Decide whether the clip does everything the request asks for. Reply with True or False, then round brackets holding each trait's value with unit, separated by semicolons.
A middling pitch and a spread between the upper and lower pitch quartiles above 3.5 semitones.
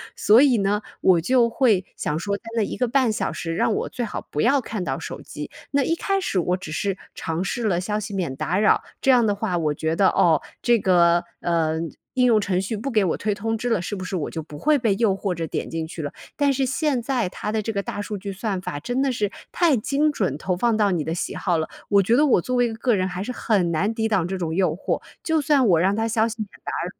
False (205 Hz; 5.0 semitones)